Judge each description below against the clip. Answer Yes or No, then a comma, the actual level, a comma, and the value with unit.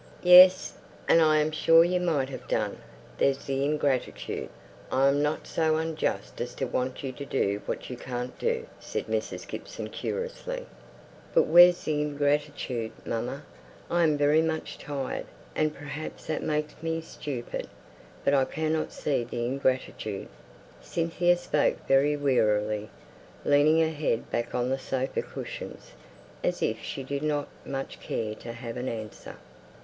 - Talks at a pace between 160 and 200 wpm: No, average, 150 wpm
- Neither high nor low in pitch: Yes, medium, 145 Hz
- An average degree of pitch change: Yes, average, 3.6 semitones